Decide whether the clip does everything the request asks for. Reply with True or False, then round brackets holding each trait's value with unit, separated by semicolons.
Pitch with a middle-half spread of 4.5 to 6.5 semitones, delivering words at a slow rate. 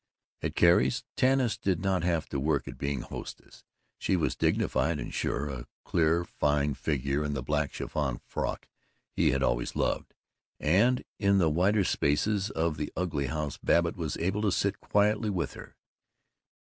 False (5.3 semitones; 165 wpm)